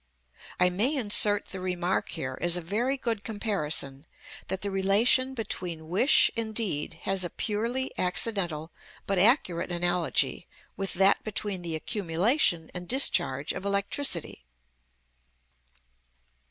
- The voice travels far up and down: No, average, 3.9 semitones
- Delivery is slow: Yes, slow, 125 wpm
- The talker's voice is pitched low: No, high, 195 Hz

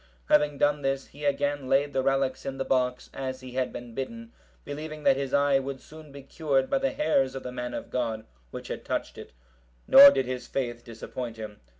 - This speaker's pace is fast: Yes, fast, 215 wpm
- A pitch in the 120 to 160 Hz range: Yes, low, 135 Hz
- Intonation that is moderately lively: No, narrow, 2.1 semitones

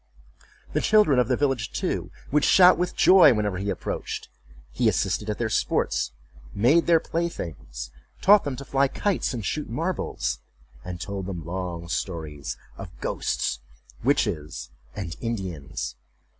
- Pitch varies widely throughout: Yes, wide, 8.8 semitones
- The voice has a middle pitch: No, low, 105 Hz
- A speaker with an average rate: Yes, average, 145 wpm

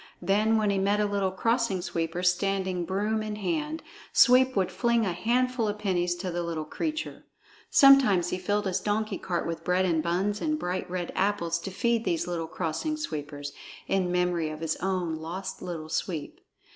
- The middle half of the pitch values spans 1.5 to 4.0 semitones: Yes, average, 3.7 semitones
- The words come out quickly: No, average, 185 wpm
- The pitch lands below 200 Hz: Yes, high, 190 Hz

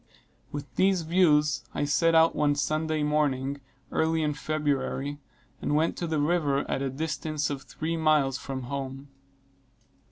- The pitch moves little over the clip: Yes, narrow, 2.2 semitones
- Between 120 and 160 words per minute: Yes, average, 150 wpm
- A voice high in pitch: No, medium, 150 Hz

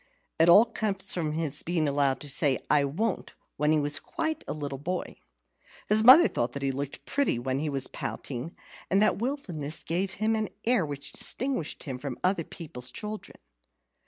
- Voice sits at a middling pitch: Yes, medium, 155 Hz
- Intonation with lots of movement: Yes, wide, 7.0 semitones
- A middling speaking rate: Yes, average, 180 wpm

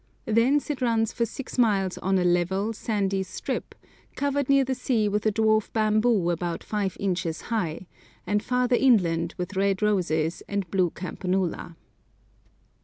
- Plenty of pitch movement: No, average, 3.9 semitones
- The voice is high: Yes, high, 205 Hz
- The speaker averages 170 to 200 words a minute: No, average, 150 wpm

